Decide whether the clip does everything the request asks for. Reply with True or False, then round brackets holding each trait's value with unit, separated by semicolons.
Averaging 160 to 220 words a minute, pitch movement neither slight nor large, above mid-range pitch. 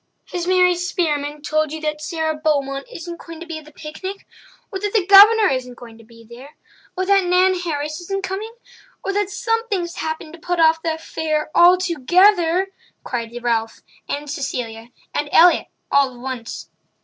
True (175 wpm; 4.3 semitones; 320 Hz)